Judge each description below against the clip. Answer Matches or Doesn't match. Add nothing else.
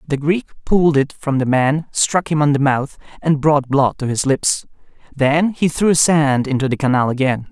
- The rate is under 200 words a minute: Doesn't match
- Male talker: Matches